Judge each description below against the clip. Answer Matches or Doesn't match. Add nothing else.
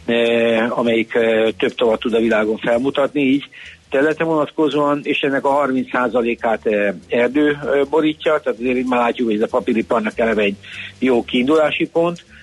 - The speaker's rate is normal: Doesn't match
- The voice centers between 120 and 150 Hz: Matches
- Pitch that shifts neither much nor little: Matches